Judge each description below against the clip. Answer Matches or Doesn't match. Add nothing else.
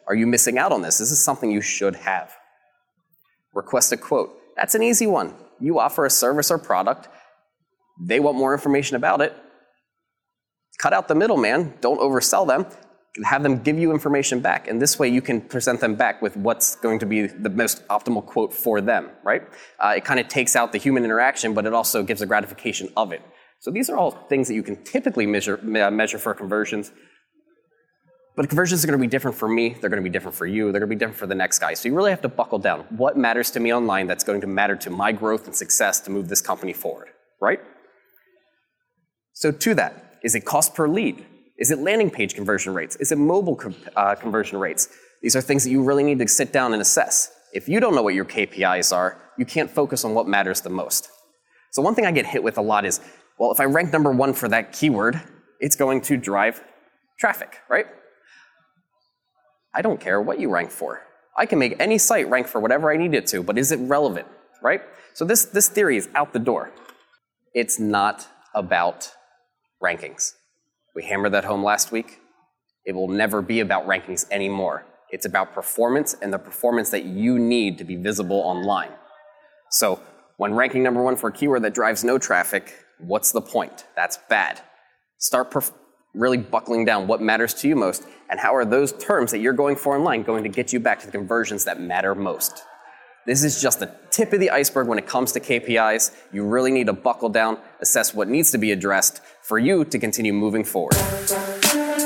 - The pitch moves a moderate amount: Doesn't match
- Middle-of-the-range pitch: Doesn't match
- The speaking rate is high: Matches